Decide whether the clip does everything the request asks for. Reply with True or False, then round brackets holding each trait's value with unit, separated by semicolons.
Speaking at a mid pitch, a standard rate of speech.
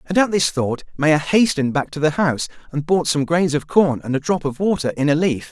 False (155 Hz; 260 wpm)